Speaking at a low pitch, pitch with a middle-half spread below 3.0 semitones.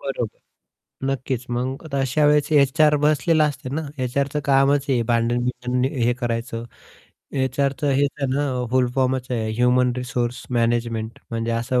Yes: low, 130 Hz; narrow, 2.6 semitones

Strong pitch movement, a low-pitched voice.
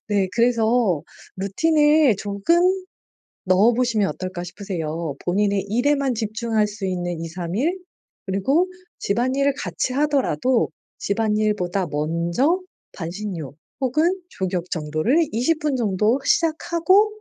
No: wide, 6.6 semitones; high, 210 Hz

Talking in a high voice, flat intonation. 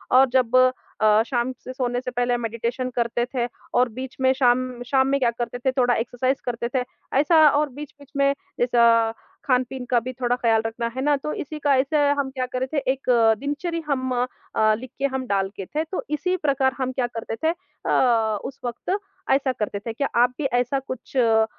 Yes: very high, 255 Hz; narrow, 2.3 semitones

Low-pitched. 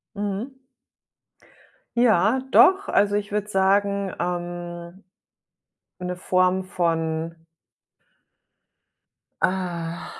No: medium, 185 Hz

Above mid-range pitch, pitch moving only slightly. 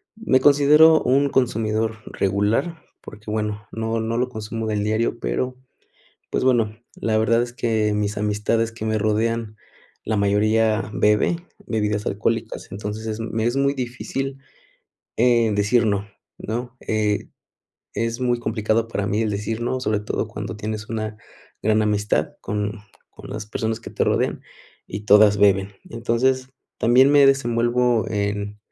No: low, 110 Hz; narrow, 2.2 semitones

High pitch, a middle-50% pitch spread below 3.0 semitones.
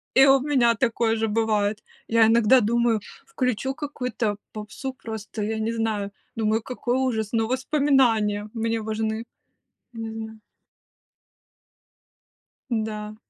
Yes: high, 225 Hz; narrow, 2.5 semitones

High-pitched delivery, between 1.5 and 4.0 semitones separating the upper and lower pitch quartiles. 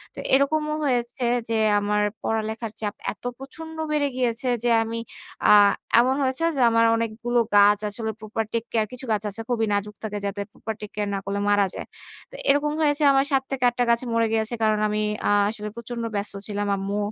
Yes: high, 225 Hz; average, 3.6 semitones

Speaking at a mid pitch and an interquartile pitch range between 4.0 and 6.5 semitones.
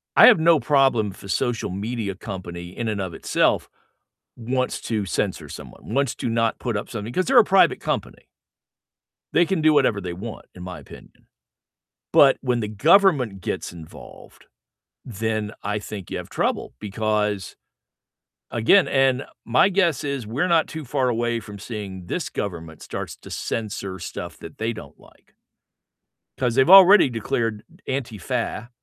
No: low, 115 Hz; average, 4.9 semitones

